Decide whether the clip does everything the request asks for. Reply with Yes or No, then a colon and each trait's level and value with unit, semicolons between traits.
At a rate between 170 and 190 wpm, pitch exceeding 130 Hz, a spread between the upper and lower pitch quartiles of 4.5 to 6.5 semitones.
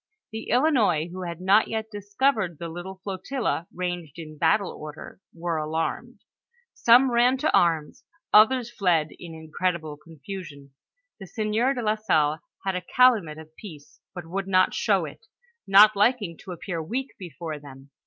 No: average, 155 wpm; medium, 185 Hz; average, 5.2 semitones